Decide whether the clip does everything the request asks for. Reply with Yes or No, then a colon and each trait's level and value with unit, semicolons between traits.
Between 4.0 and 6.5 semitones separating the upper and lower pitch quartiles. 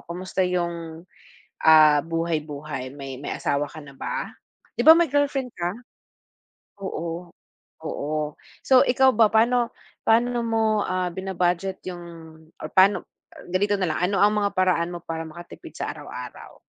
Yes: average, 4.7 semitones